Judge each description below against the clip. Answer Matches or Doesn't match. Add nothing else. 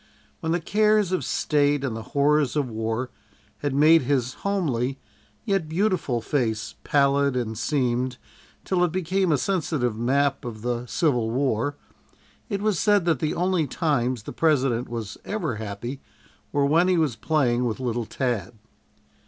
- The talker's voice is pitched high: Doesn't match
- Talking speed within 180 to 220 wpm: Doesn't match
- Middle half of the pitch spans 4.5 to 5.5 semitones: Matches